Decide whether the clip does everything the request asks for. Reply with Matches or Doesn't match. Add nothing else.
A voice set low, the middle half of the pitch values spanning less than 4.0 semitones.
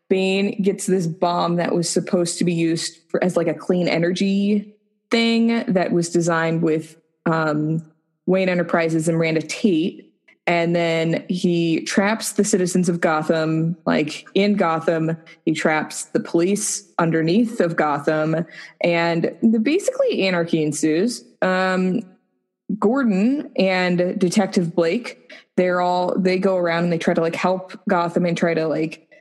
Doesn't match